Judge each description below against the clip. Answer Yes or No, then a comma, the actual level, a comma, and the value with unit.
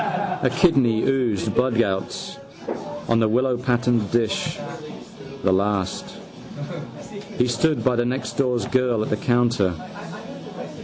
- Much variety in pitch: No, average, 2.7 semitones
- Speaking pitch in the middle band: No, low, 120 Hz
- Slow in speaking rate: Yes, slow, 105 wpm